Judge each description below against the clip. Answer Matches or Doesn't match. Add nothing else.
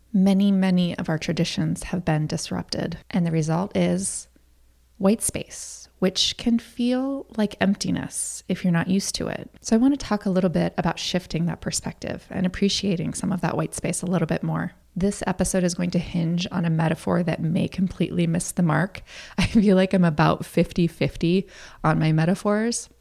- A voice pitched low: Doesn't match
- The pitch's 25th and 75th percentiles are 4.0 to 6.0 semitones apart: Doesn't match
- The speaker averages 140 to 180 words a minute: Doesn't match